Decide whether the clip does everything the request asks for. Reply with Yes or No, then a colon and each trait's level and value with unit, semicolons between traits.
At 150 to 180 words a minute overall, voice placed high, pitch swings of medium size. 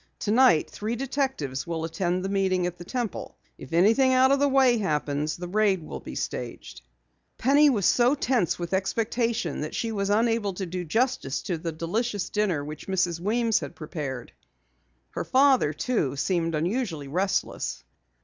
No: average, 165 wpm; high, 195 Hz; wide, 6.2 semitones